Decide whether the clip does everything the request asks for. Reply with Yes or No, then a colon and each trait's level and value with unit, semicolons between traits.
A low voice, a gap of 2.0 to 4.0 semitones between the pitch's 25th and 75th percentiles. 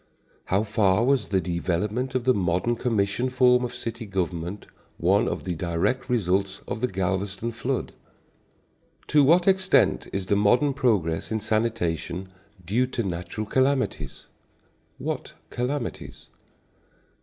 No: low, 110 Hz; average, 5.0 semitones